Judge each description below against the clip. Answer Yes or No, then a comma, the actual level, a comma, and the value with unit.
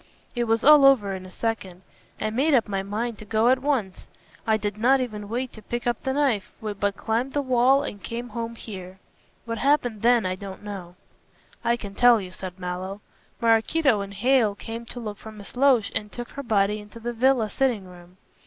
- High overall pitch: Yes, high, 225 Hz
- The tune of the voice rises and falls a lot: No, average, 3.4 semitones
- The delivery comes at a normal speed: No, fast, 210 wpm